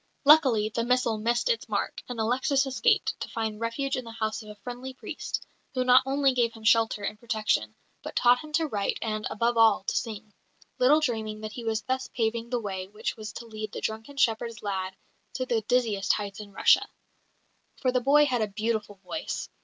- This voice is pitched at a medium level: No, high, 230 Hz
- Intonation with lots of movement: No, average, 2.8 semitones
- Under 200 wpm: No, fast, 205 wpm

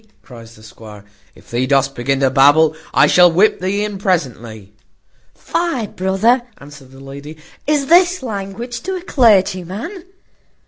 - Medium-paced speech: Yes, average, 145 wpm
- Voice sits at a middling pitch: Yes, medium, 180 Hz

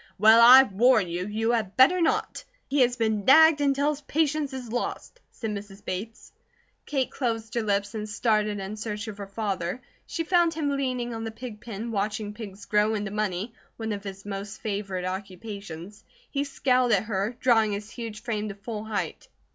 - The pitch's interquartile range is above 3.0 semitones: Yes, average, 3.5 semitones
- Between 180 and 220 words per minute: Yes, average, 185 wpm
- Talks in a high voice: Yes, high, 220 Hz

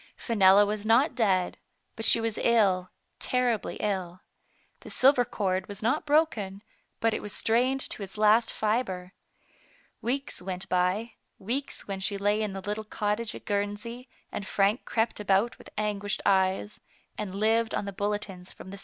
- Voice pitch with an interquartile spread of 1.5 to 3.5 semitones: Yes, average, 2.8 semitones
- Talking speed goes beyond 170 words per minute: No, average, 165 wpm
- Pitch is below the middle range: No, high, 210 Hz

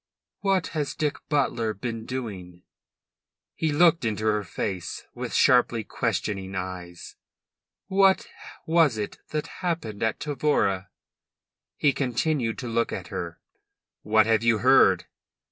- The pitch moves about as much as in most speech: No, wide, 6.3 semitones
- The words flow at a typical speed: No, slow, 125 wpm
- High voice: No, low, 115 Hz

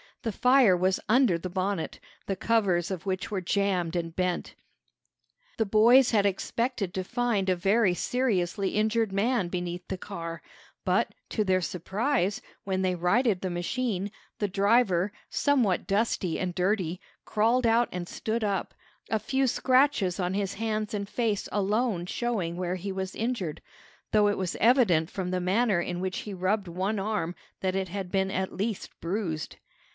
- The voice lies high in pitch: Yes, high, 195 Hz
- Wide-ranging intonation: No, average, 3.4 semitones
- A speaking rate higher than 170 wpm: No, average, 165 wpm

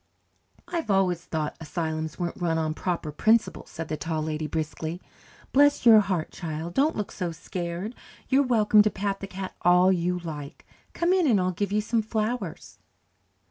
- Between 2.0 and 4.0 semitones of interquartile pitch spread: No, average, 4.7 semitones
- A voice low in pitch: No, medium, 180 Hz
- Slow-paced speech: No, average, 175 wpm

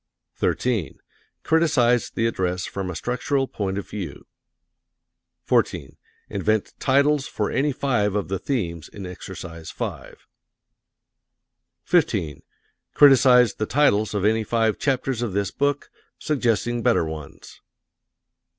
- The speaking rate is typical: No, slow, 115 wpm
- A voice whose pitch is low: Yes, low, 110 Hz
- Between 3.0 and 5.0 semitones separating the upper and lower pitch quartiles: No, wide, 5.4 semitones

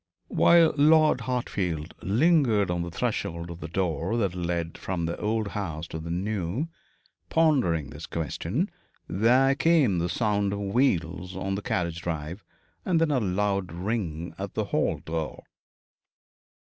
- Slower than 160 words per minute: Yes, average, 145 wpm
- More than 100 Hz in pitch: No, very low, 95 Hz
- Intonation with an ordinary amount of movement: No, wide, 5.7 semitones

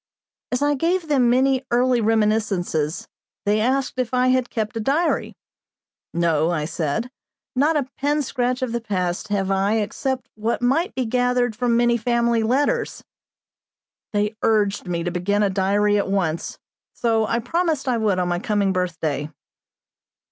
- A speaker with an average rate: Yes, average, 160 wpm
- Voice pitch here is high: Yes, high, 225 Hz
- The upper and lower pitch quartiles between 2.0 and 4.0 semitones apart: No, average, 4.6 semitones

